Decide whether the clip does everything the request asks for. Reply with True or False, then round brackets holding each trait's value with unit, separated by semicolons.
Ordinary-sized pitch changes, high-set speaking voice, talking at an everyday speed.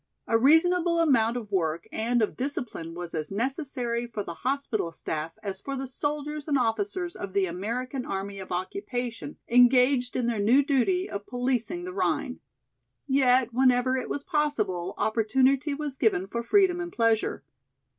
True (4.8 semitones; 250 Hz; 160 wpm)